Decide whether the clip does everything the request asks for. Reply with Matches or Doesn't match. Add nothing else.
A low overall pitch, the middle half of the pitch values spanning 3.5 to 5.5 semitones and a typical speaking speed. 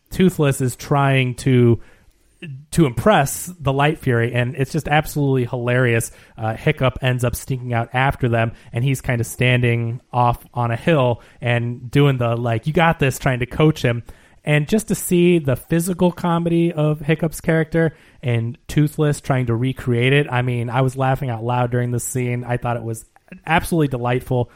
Matches